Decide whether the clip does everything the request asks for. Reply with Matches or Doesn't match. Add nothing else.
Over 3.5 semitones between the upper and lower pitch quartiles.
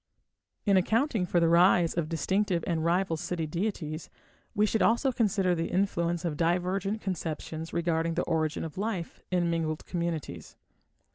Doesn't match